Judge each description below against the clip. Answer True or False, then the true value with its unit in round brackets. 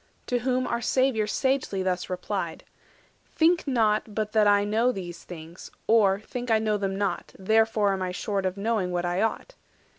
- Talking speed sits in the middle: True (185 wpm)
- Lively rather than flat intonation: False (3.3 semitones)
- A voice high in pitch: True (210 Hz)